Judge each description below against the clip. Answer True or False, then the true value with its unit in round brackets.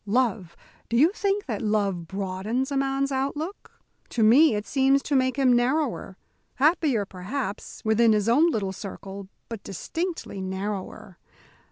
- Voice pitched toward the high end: True (235 Hz)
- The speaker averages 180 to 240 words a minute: False (145 wpm)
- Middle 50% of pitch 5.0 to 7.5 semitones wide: True (5.6 semitones)